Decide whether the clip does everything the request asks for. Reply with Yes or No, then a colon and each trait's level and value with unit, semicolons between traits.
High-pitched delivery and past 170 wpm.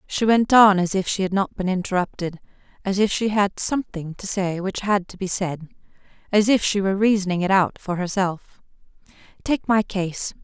Yes: high, 195 Hz; average, 195 wpm